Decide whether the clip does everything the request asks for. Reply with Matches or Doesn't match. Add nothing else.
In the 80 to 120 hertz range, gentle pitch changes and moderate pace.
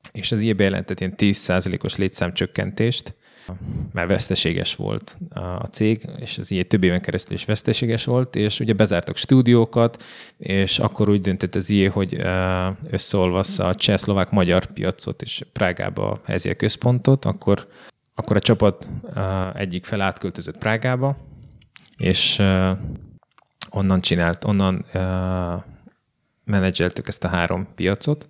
Doesn't match